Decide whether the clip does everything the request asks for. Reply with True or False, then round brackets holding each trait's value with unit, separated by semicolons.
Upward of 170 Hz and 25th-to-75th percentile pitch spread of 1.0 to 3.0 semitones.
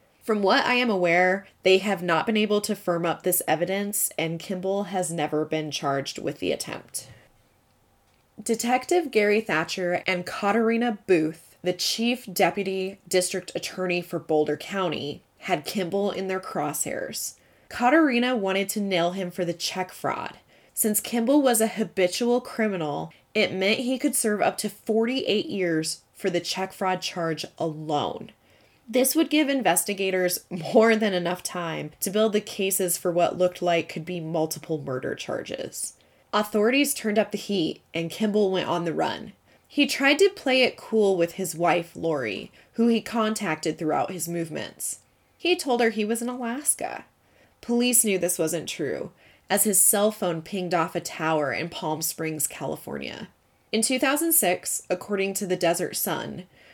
False (190 Hz; 4.3 semitones)